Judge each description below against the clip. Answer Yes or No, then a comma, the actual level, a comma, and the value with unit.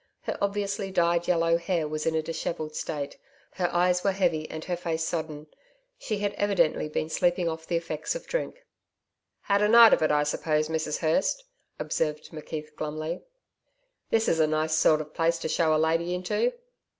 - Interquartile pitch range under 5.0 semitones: Yes, narrow, 2.6 semitones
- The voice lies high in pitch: No, medium, 165 Hz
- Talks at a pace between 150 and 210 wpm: Yes, average, 185 wpm